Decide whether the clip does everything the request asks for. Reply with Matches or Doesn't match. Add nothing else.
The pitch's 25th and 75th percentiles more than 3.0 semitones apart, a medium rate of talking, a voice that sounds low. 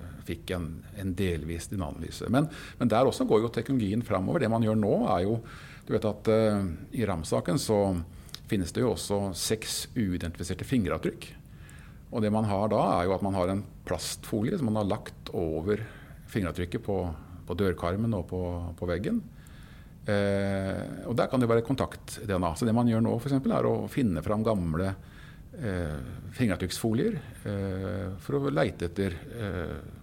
Matches